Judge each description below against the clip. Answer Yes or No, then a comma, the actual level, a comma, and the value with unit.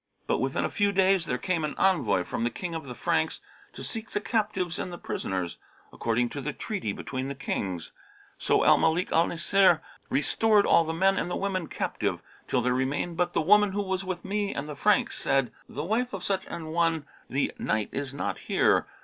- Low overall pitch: No, medium, 170 Hz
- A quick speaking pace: Yes, fast, 210 wpm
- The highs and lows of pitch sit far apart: Yes, wide, 6.0 semitones